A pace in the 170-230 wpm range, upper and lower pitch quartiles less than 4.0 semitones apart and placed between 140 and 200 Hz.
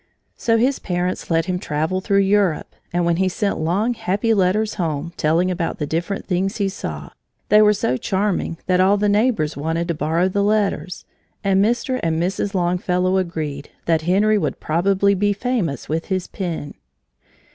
Yes: average, 175 wpm; average, 3.5 semitones; medium, 185 Hz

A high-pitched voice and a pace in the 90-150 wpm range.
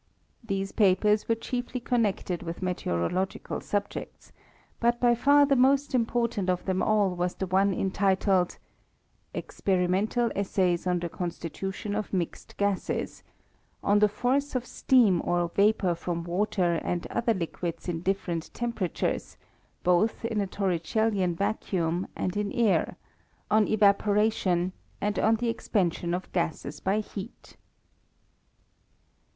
Yes: high, 195 Hz; slow, 135 wpm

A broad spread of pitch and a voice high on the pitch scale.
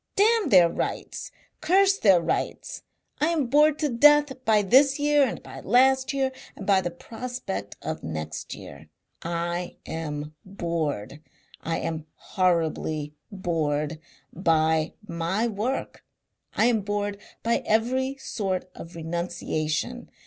Yes: wide, 8.1 semitones; high, 195 Hz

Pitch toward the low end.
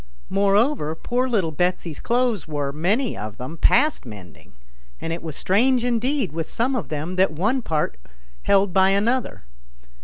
No: high, 190 Hz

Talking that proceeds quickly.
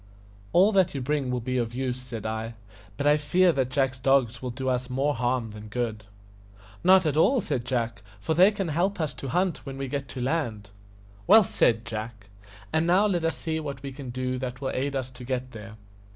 Yes: fast, 220 wpm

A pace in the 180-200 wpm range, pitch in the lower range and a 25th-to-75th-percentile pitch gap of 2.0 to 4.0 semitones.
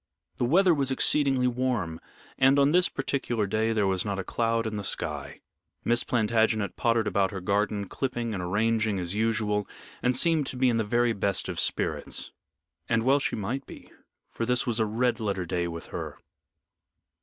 Yes: average, 185 wpm; low, 115 Hz; average, 3.7 semitones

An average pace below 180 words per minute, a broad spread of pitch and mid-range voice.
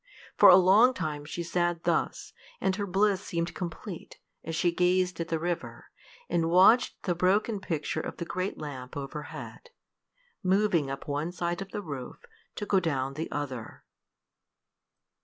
No: average, 160 wpm; average, 3.4 semitones; medium, 175 Hz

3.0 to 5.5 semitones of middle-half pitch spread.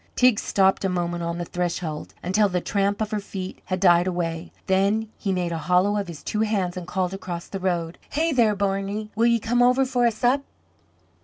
Yes: average, 3.4 semitones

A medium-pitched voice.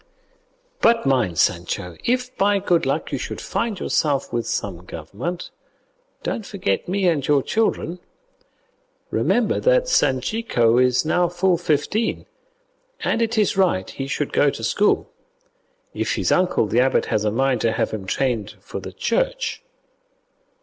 Yes: medium, 155 Hz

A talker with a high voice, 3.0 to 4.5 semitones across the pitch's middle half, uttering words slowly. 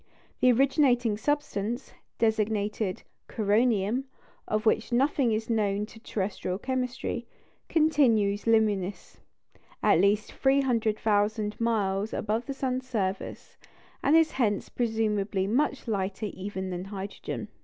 Yes: high, 220 Hz; average, 3.5 semitones; slow, 110 wpm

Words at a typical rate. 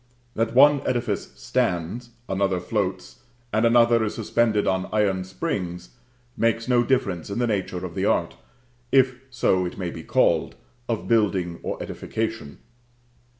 Yes: average, 145 wpm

